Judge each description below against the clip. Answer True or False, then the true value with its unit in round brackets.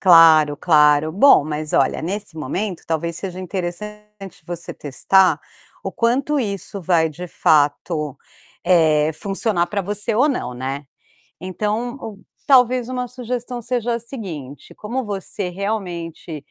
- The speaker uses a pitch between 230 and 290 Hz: False (190 Hz)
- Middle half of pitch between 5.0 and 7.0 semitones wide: True (5.6 semitones)